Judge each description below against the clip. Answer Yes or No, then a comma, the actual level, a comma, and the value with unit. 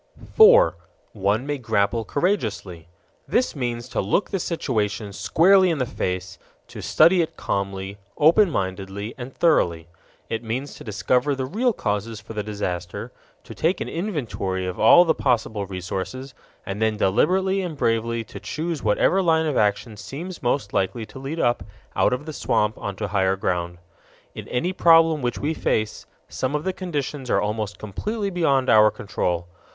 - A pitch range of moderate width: No, wide, 7.9 semitones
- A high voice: No, low, 120 Hz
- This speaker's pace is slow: No, average, 165 wpm